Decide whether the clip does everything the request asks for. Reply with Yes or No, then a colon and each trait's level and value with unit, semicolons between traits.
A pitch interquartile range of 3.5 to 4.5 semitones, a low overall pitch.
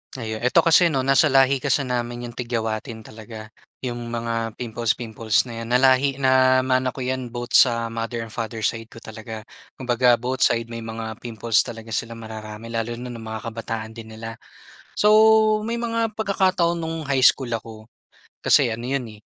No: narrow, 2.5 semitones; low, 120 Hz